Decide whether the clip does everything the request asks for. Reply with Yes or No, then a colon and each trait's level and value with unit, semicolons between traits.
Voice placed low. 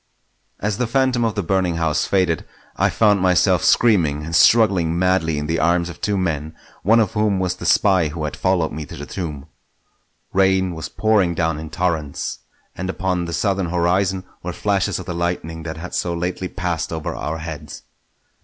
Yes: very low, 90 Hz